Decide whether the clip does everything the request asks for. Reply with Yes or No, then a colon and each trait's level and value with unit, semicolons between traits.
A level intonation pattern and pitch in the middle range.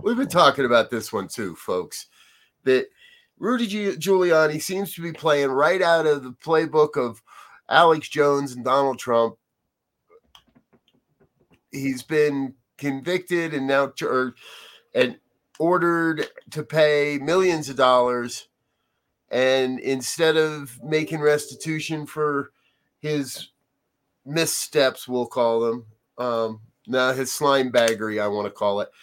No: average, 4.4 semitones; medium, 150 Hz